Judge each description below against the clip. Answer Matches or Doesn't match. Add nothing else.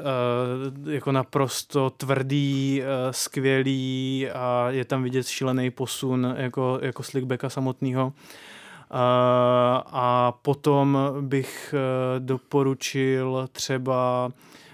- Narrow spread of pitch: Matches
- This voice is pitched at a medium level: Doesn't match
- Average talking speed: Doesn't match